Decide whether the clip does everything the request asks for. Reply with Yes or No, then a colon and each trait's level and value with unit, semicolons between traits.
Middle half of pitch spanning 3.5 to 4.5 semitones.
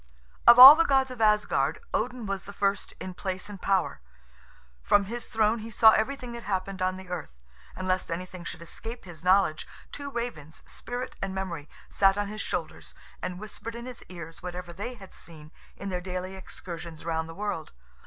Yes: average, 3.9 semitones